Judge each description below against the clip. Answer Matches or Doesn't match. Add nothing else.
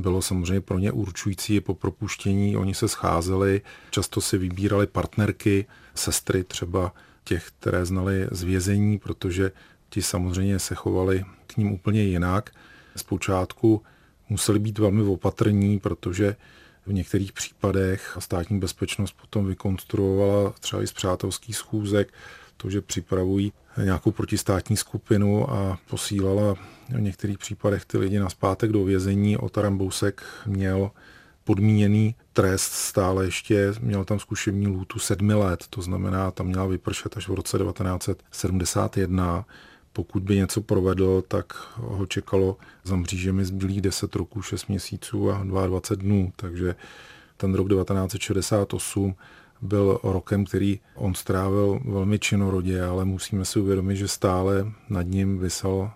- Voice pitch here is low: Matches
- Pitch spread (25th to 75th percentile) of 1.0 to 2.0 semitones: Matches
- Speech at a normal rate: Matches